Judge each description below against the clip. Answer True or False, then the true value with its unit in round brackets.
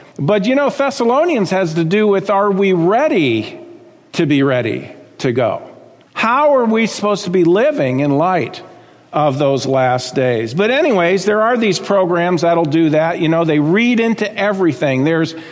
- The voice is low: False (190 Hz)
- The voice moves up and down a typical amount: False (5.9 semitones)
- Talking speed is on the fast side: False (175 wpm)